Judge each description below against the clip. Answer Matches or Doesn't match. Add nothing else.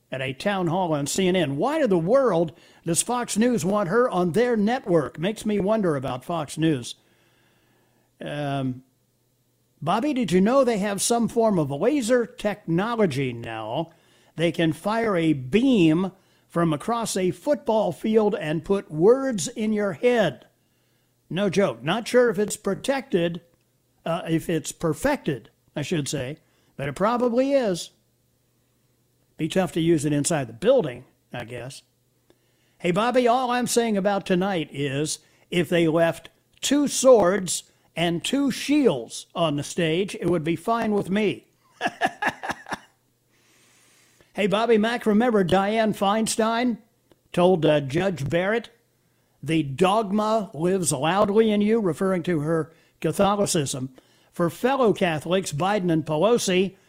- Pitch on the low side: Doesn't match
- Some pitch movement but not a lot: Doesn't match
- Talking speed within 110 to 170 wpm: Matches